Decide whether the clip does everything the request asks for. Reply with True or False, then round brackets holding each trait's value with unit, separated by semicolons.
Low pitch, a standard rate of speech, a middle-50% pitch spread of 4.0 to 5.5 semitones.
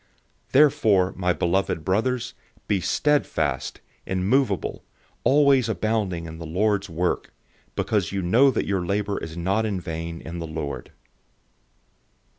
False (95 Hz; 130 wpm; 4.8 semitones)